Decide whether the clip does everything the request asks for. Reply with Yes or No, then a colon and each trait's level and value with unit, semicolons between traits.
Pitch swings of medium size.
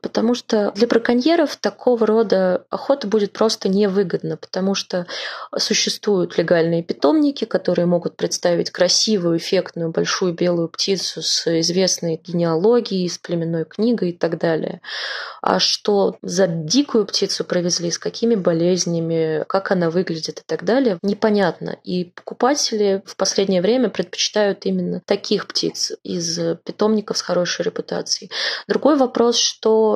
Yes: average, 4.1 semitones